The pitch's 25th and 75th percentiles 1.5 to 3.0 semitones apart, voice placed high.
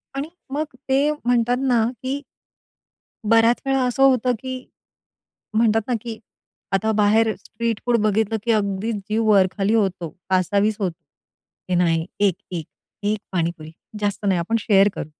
No: average, 3.5 semitones; high, 215 Hz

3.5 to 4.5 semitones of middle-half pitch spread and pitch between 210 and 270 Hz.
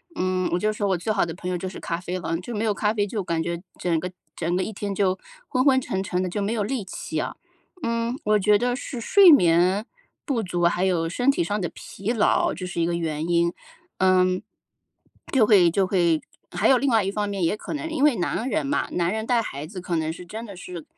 No: average, 4.0 semitones; high, 190 Hz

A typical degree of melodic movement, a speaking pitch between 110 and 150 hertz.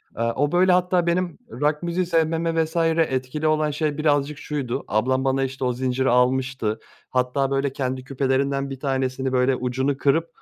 Yes: average, 3.2 semitones; low, 135 Hz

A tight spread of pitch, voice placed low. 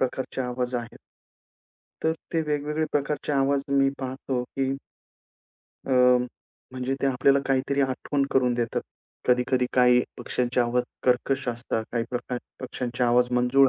Yes: narrow, 1.8 semitones; low, 130 Hz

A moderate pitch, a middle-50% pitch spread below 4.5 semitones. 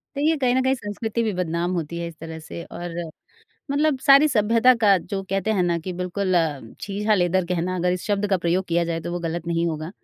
Yes: medium, 180 Hz; average, 3.8 semitones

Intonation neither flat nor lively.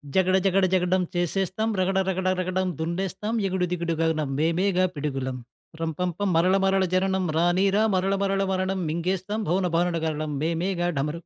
No: narrow, 2.3 semitones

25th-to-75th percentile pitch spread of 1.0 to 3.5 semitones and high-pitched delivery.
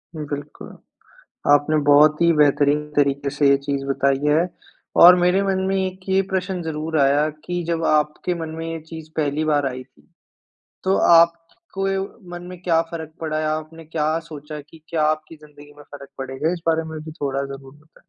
No: narrow, 2.5 semitones; medium, 155 Hz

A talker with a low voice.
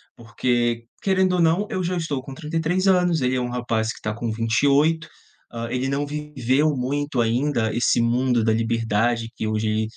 Yes: low, 125 Hz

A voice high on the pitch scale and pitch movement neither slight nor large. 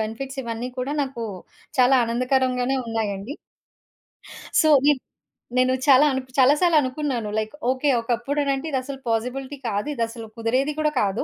Yes: very high, 255 Hz; average, 3.0 semitones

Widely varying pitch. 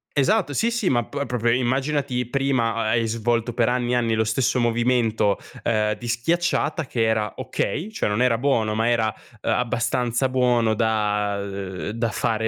No: narrow, 2.4 semitones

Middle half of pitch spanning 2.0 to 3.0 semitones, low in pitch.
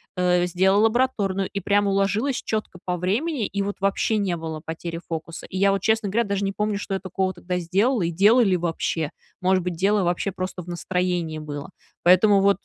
No: narrow, 2.6 semitones; high, 190 Hz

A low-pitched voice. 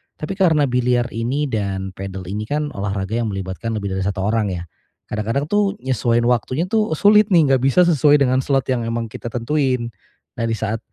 Yes: low, 120 Hz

